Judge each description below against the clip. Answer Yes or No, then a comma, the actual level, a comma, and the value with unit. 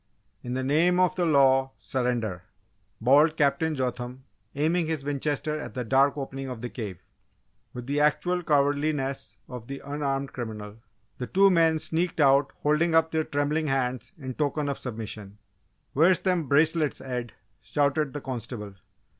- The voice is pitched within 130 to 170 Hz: Yes, medium, 140 Hz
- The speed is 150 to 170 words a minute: Yes, average, 155 wpm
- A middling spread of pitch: Yes, average, 3.6 semitones